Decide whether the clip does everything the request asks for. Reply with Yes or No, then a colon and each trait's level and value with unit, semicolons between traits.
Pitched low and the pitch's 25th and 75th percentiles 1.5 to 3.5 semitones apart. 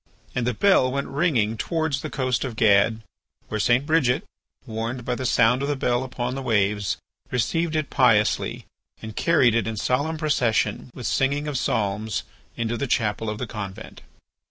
No: low, 125 Hz; average, 3.9 semitones